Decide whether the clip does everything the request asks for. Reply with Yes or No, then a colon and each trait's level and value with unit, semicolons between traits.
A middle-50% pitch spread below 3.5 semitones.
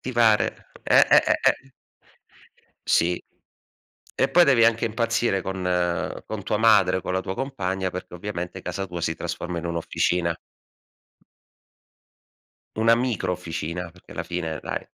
No: average, 4.4 semitones